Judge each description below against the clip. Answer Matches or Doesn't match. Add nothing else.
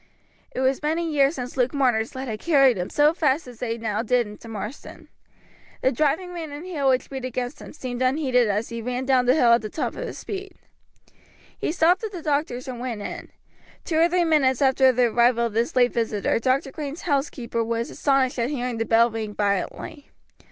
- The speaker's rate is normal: Doesn't match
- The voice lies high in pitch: Matches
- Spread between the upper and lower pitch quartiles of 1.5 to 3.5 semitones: Doesn't match